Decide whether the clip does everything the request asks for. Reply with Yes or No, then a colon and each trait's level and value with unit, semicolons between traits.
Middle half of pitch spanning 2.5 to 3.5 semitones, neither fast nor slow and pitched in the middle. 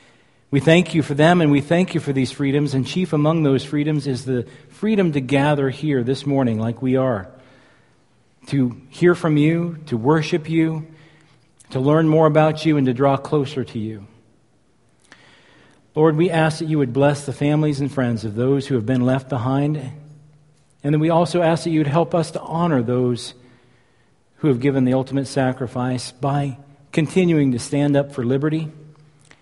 Yes: average, 3.2 semitones; average, 185 wpm; medium, 145 Hz